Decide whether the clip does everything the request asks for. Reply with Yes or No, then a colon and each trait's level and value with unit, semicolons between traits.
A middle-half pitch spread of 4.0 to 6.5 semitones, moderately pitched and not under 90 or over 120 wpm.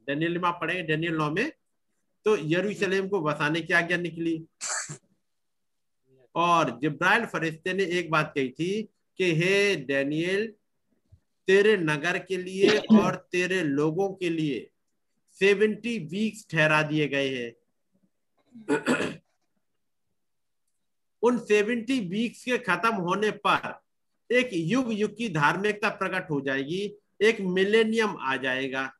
Yes: average, 5.1 semitones; medium, 180 Hz; average, 115 wpm